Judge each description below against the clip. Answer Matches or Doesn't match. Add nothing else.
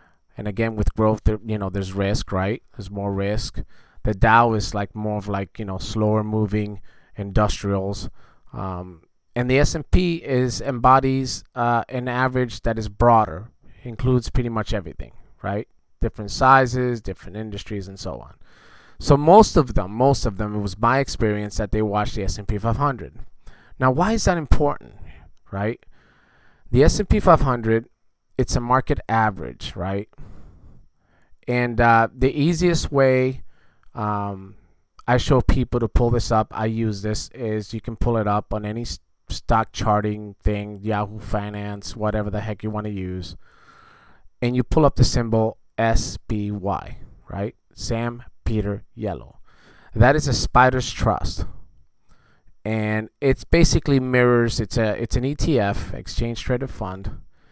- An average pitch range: Matches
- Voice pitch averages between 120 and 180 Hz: Doesn't match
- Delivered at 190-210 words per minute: Doesn't match